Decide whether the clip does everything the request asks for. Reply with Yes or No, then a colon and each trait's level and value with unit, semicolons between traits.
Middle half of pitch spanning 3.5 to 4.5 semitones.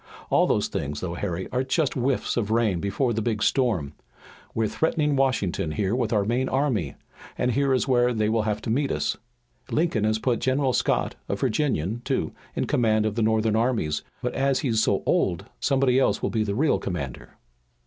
Yes: average, 3.8 semitones